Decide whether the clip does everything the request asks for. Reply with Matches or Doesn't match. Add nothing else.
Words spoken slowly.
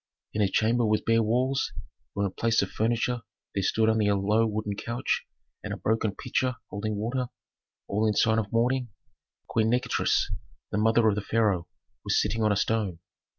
Doesn't match